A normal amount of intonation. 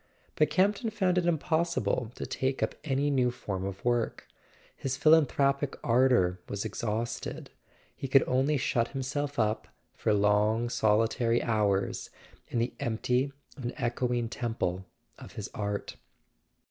Yes: average, 4.1 semitones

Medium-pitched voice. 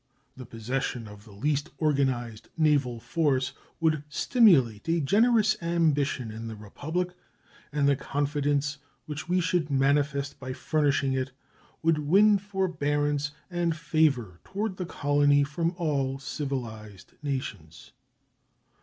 Yes: medium, 145 Hz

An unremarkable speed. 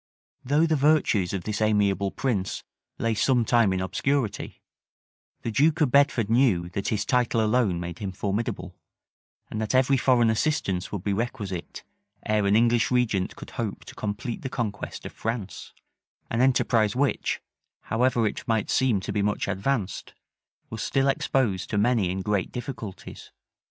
Yes: average, 160 wpm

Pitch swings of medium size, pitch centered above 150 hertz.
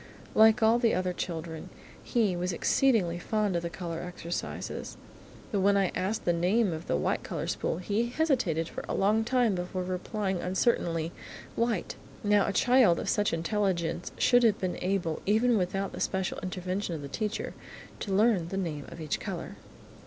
Yes: average, 4.0 semitones; high, 190 Hz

